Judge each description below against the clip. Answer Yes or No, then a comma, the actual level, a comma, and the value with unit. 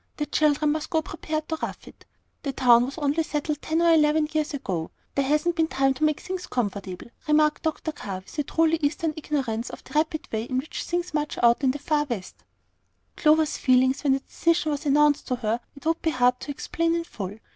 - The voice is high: Yes, very high, 295 Hz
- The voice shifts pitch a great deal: No, average, 3.4 semitones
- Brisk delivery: Yes, fast, 215 wpm